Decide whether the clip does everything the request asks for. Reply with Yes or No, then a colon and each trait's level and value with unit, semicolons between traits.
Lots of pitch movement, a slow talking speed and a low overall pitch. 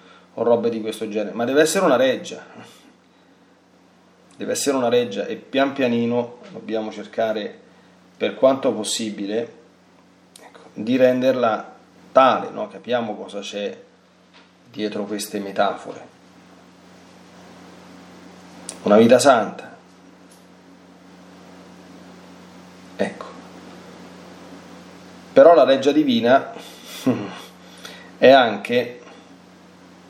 No: average, 5.0 semitones; slow, 85 wpm; low, 100 Hz